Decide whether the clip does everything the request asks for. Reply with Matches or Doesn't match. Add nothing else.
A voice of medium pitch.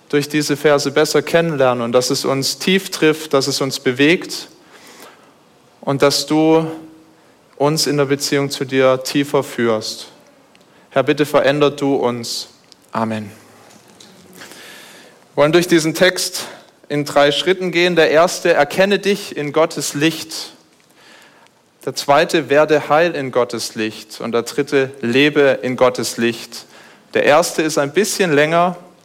Matches